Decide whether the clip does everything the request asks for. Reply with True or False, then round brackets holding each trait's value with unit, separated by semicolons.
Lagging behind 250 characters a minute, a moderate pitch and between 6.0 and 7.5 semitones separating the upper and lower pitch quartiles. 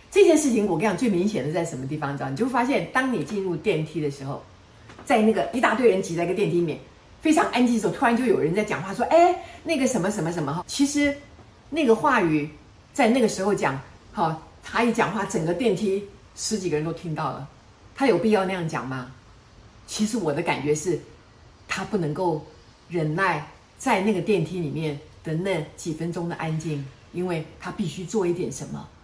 False (305 characters per minute; 175 Hz; 6.6 semitones)